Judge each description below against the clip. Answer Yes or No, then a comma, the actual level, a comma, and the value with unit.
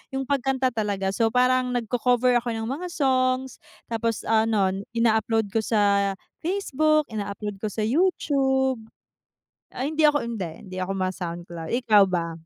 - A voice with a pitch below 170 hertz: No, high, 230 Hz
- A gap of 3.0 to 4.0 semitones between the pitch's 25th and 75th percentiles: No, average, 4.6 semitones